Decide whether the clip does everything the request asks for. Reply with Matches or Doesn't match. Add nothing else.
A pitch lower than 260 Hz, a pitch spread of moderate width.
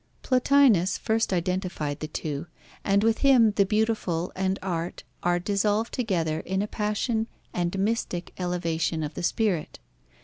Matches